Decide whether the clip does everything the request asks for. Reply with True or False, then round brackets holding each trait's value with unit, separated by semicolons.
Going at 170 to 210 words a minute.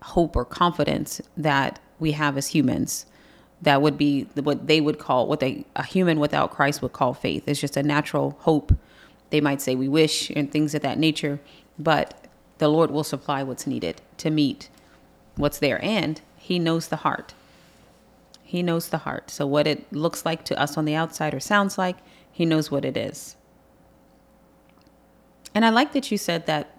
True (190 wpm)